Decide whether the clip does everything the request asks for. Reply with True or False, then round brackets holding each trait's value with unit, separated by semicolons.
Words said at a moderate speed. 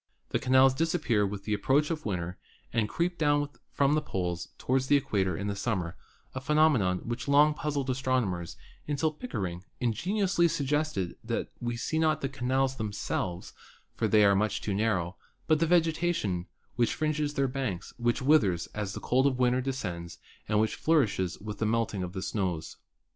True (180 wpm)